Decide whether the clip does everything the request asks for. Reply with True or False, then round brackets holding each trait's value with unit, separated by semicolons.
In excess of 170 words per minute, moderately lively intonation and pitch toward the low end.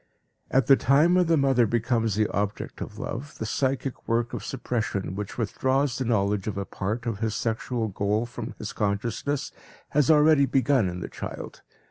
True (180 wpm; 4.4 semitones; 120 Hz)